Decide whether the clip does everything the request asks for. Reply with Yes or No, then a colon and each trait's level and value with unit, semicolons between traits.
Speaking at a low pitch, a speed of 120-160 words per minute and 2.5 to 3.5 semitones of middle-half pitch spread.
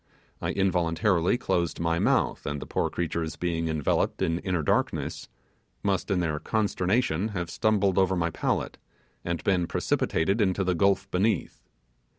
Yes: very low, 90 Hz; average, 150 wpm; average, 2.9 semitones